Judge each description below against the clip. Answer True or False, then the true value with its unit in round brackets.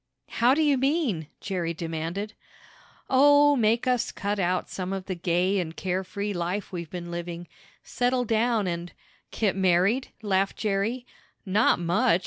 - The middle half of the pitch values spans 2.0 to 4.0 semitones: False (5.0 semitones)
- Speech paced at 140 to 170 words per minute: True (150 wpm)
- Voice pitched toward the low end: False (195 Hz)